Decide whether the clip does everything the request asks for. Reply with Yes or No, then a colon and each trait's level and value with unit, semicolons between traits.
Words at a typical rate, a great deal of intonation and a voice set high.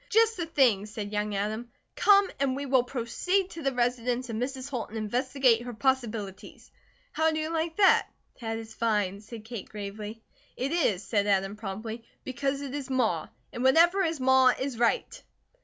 No: average, 180 wpm; average, 4.3 semitones; high, 245 Hz